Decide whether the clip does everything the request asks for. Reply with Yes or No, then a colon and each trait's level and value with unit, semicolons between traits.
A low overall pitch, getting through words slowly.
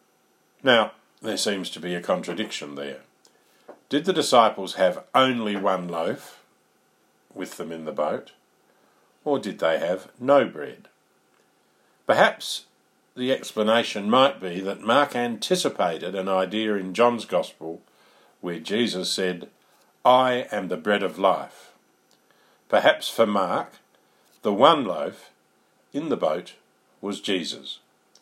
Yes: low, 100 Hz; slow, 125 wpm